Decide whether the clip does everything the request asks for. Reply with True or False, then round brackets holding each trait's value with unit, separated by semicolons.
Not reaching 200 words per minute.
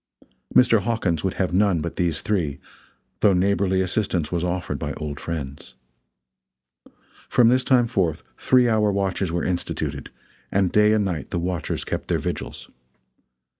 True (150 wpm)